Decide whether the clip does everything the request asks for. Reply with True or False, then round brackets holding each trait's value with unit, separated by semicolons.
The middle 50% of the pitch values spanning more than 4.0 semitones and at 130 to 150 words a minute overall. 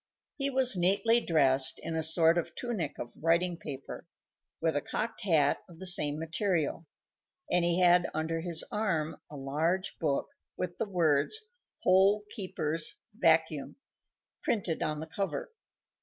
False (3.3 semitones; 145 wpm)